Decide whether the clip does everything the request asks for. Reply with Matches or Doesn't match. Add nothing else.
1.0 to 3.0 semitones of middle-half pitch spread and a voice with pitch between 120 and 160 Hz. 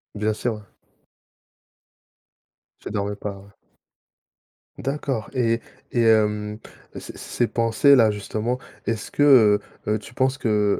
Doesn't match